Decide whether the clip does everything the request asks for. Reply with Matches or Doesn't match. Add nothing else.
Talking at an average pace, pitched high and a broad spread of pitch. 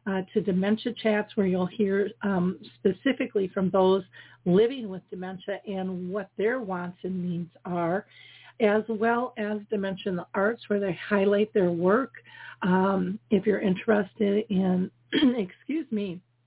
Doesn't match